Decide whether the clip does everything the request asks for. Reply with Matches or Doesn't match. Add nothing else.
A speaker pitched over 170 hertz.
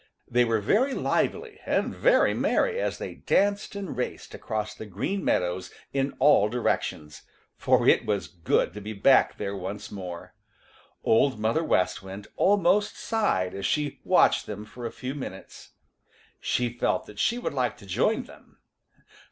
Doesn't match